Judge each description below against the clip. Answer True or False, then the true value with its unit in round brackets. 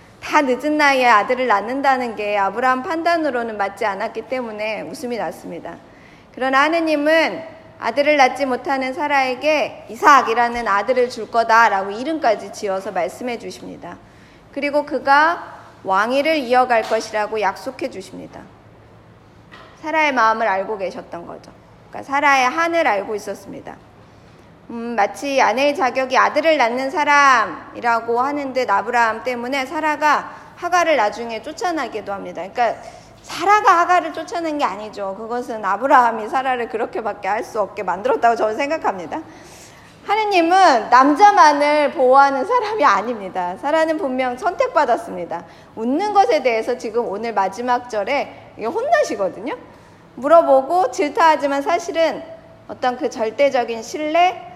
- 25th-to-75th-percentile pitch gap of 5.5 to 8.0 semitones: False (5.1 semitones)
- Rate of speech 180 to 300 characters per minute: False (335 characters per minute)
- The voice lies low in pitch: False (260 Hz)